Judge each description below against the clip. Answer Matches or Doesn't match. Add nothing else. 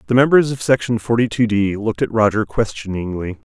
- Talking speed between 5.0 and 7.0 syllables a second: Matches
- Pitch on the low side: Matches